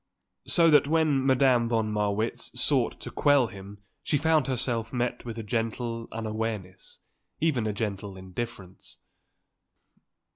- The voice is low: Yes, low, 115 Hz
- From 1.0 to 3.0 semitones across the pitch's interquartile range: No, average, 3.9 semitones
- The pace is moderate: No, slow, 130 wpm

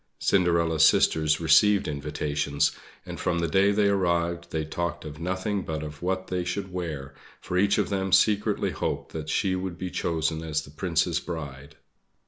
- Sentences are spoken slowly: No, average, 170 wpm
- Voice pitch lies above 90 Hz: No, very low, 85 Hz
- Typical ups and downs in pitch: Yes, average, 3.3 semitones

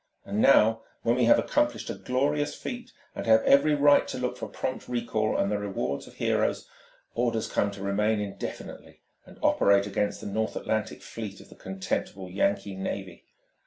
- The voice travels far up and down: No, average, 4.0 semitones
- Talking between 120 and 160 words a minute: No, average, 175 wpm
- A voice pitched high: No, low, 110 Hz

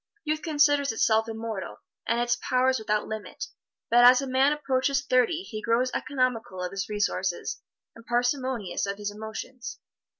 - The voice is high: Yes, high, 240 Hz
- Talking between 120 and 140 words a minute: No, average, 155 wpm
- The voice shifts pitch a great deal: No, average, 3.4 semitones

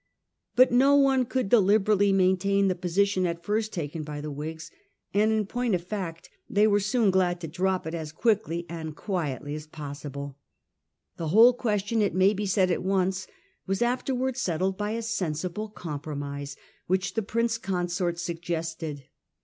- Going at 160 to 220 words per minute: Yes, average, 170 wpm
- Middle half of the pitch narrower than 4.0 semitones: No, average, 4.5 semitones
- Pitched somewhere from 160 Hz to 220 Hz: Yes, medium, 185 Hz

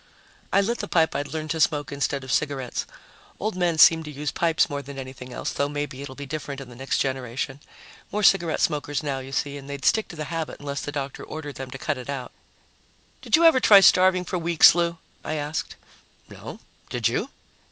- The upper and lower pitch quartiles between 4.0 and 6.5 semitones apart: No, average, 3.4 semitones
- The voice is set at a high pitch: No, medium, 145 Hz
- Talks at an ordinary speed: No, fast, 215 wpm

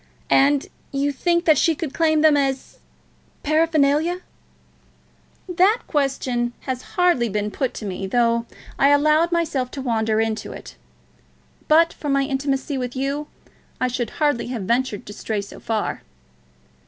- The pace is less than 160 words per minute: Yes, average, 145 wpm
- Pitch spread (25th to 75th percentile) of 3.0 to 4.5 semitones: Yes, average, 4.2 semitones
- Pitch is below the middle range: No, very high, 275 Hz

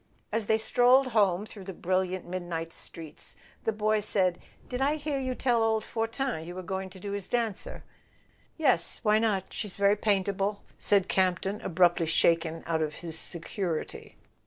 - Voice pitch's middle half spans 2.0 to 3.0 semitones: No, average, 3.9 semitones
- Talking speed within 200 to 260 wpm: No, average, 170 wpm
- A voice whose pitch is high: Yes, high, 200 Hz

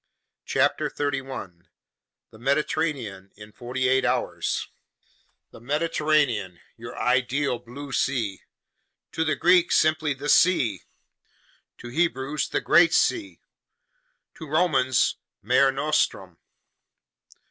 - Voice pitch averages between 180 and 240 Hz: No, low, 135 Hz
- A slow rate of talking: Yes, slow, 95 wpm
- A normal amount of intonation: Yes, average, 4.2 semitones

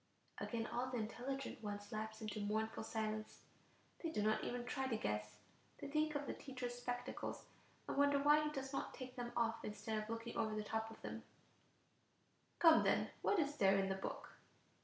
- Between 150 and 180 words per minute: No, average, 190 wpm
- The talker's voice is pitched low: No, high, 230 Hz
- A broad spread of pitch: No, average, 3.8 semitones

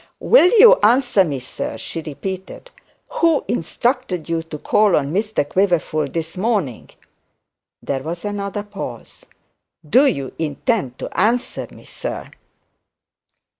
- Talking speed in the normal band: No, slow, 125 wpm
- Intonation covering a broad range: Yes, wide, 6.9 semitones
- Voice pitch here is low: No, high, 190 Hz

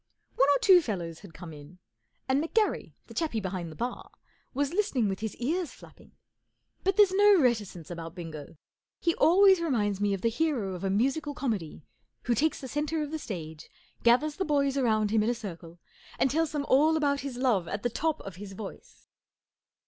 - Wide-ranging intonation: Yes, wide, 7.9 semitones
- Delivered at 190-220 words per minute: Yes, average, 195 wpm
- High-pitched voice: Yes, high, 245 Hz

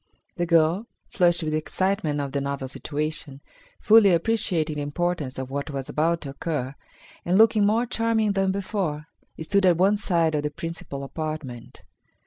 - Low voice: No, medium, 165 Hz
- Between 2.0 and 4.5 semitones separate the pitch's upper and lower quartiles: No, average, 4.9 semitones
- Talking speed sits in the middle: Yes, average, 160 wpm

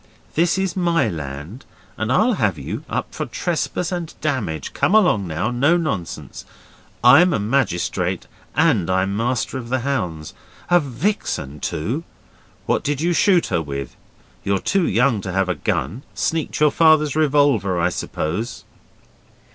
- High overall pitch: No, low, 125 Hz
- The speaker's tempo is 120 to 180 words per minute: Yes, average, 150 wpm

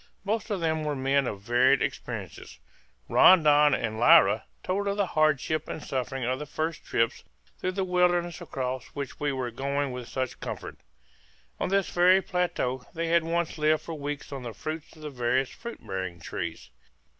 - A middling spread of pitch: Yes, average, 4.8 semitones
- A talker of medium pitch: Yes, medium, 145 Hz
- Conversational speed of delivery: Yes, average, 180 wpm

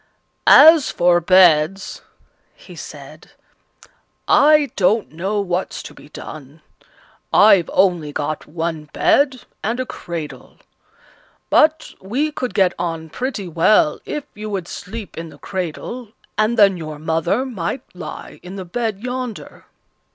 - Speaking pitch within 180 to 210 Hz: Yes, high, 190 Hz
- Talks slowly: Yes, slow, 130 wpm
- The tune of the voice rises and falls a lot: Yes, wide, 6.1 semitones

